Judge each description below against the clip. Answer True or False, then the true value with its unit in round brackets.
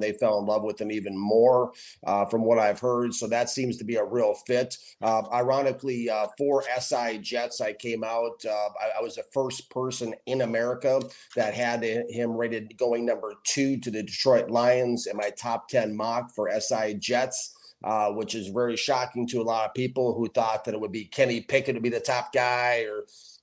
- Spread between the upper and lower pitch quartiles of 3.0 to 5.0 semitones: False (2.4 semitones)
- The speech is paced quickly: True (210 wpm)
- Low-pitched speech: True (120 Hz)